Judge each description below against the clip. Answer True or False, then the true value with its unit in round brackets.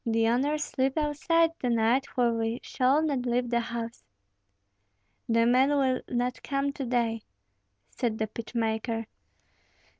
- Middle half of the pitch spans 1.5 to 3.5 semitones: True (3.0 semitones)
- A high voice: True (245 Hz)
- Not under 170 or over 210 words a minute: False (145 wpm)